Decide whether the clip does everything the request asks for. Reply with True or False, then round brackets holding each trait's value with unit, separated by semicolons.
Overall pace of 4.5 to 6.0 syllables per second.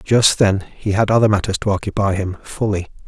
True (5.5 syllables/s)